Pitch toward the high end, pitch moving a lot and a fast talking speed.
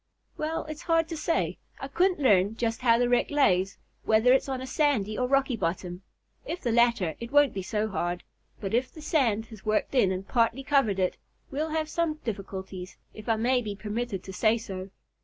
Yes: high, 235 Hz; wide, 5.7 semitones; fast, 210 wpm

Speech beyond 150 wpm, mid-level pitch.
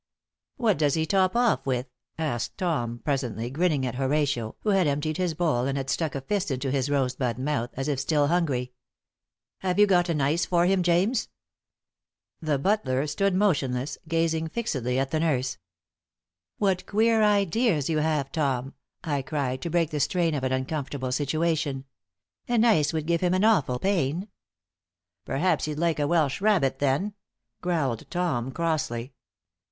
Yes: average, 165 wpm; medium, 155 Hz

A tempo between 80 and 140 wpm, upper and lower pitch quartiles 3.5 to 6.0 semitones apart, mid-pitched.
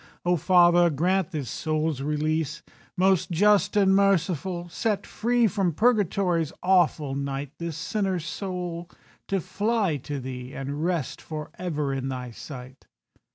Yes: slow, 135 wpm; average, 4.7 semitones; medium, 170 Hz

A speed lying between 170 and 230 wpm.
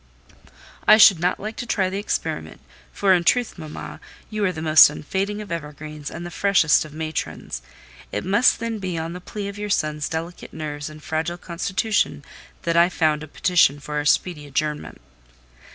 Yes: average, 185 wpm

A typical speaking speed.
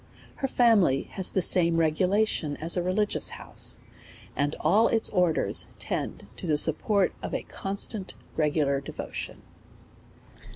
No: slow, 130 wpm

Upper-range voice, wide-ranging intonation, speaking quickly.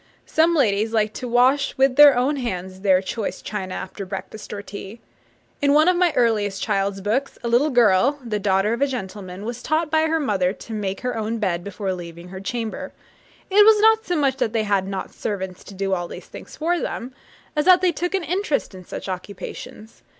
Yes: high, 220 Hz; wide, 6.7 semitones; fast, 210 wpm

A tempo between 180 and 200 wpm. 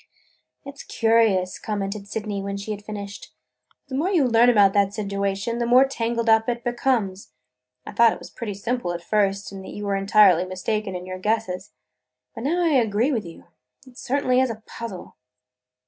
Yes: average, 190 wpm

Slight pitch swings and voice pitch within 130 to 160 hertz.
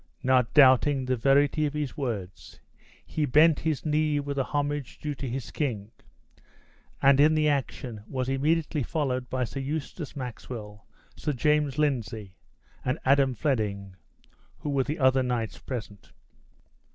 No: average, 3.0 semitones; low, 135 Hz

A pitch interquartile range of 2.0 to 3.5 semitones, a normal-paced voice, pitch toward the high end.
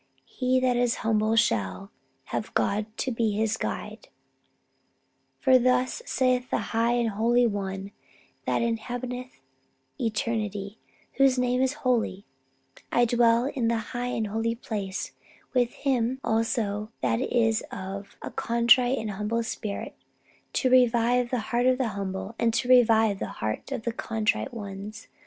Yes: average, 2.7 semitones; average, 145 wpm; high, 230 Hz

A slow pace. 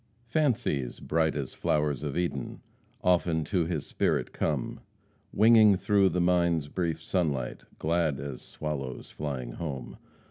Yes: slow, 130 wpm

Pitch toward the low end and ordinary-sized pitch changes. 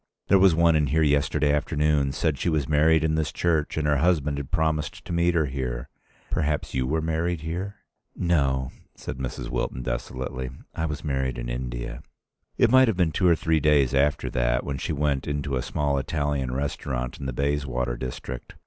Yes: very low, 75 Hz; average, 3.3 semitones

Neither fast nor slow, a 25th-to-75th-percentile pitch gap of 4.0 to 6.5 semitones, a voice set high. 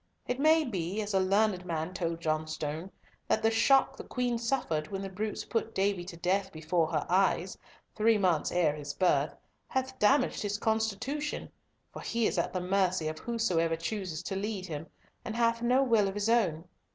Yes: average, 190 wpm; average, 5.1 semitones; high, 195 Hz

